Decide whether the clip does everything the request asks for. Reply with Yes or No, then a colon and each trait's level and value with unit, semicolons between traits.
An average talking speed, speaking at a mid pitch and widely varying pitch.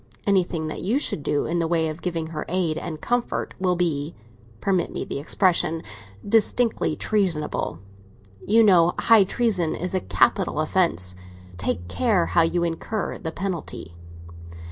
No: average, 145 wpm; medium, 170 Hz; average, 4.0 semitones